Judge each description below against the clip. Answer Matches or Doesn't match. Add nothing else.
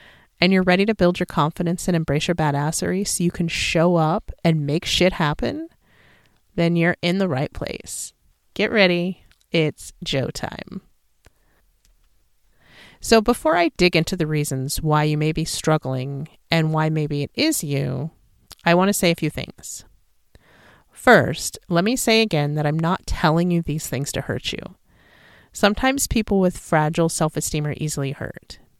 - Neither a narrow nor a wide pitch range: Matches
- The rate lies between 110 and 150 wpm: Doesn't match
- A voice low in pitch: Doesn't match